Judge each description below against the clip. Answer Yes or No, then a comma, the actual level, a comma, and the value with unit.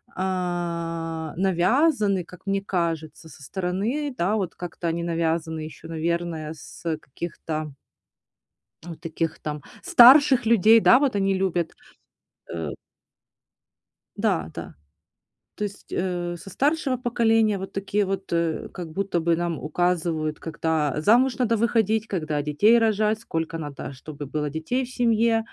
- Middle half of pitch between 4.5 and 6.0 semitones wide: Yes, average, 5.1 semitones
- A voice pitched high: No, medium, 175 Hz